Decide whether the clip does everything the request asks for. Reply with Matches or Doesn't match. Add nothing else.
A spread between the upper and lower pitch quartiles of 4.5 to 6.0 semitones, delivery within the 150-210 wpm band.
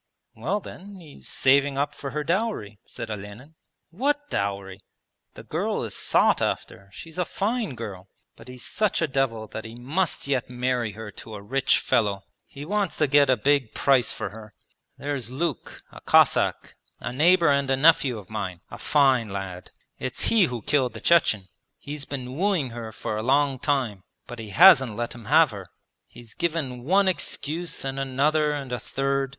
Matches